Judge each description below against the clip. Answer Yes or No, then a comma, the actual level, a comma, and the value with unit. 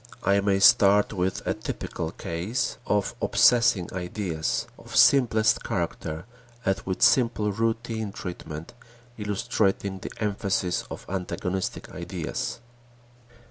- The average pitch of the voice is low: Yes, low, 100 Hz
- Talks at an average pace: No, slow, 105 wpm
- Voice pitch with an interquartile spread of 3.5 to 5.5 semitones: No, average, 3.1 semitones